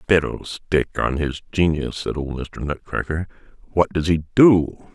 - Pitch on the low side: Yes, very low, 80 Hz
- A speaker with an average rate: Yes, average, 145 wpm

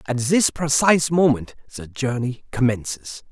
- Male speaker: Yes, male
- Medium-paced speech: No, slow, 125 wpm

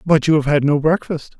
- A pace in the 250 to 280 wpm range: Yes, fast, 260 wpm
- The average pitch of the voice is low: No, medium, 150 Hz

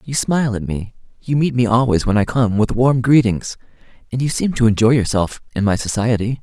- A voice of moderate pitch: No, low, 115 Hz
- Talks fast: Yes, fast, 215 wpm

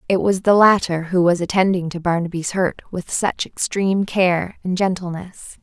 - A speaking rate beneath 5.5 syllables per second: Yes, 4.8 syllables/s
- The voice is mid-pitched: Yes, medium, 180 Hz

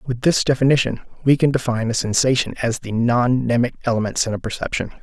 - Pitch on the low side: Yes, low, 125 Hz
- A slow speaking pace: No, average, 190 wpm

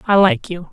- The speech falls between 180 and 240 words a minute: No, fast, 250 wpm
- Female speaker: Yes, female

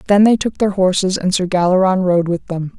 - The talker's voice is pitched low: No, medium, 185 Hz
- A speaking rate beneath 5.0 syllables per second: No, 5.6 syllables/s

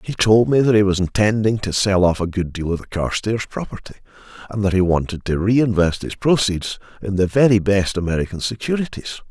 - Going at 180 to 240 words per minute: Yes, average, 200 wpm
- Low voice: Yes, low, 100 Hz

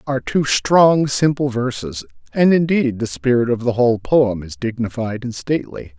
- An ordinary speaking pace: Yes, average, 170 wpm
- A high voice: No, low, 125 Hz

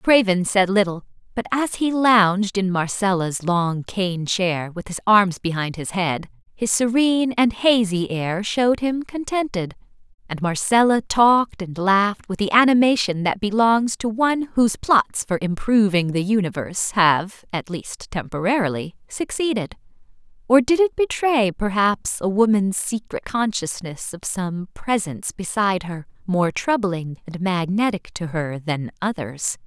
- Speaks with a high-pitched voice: Yes, high, 200 Hz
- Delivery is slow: No, average, 145 wpm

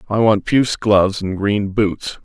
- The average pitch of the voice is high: No, low, 105 Hz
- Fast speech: No, average, 190 wpm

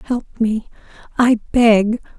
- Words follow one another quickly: No, slow, 110 wpm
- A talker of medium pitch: No, high, 225 Hz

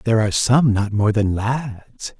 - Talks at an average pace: Yes, average, 190 wpm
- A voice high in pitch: No, low, 110 Hz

